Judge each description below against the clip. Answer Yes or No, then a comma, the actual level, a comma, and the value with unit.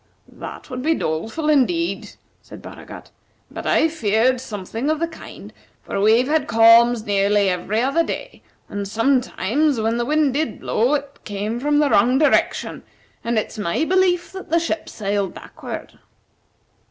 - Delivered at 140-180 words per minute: Yes, average, 155 wpm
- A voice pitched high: Yes, very high, 250 Hz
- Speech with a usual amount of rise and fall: No, wide, 6.1 semitones